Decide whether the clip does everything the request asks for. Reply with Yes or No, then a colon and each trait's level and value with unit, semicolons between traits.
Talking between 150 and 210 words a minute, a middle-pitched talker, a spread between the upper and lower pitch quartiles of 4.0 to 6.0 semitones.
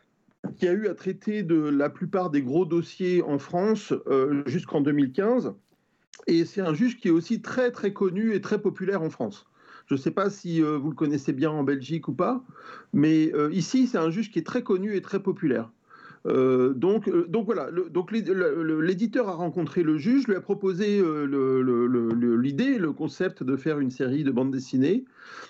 Yes: average, 205 wpm; medium, 175 Hz; average, 5.2 semitones